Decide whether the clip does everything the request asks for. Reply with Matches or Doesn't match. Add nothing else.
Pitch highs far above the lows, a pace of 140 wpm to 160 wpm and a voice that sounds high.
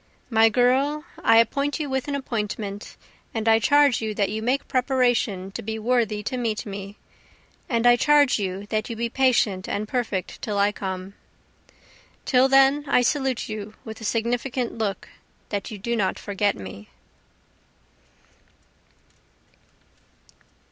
Doesn't match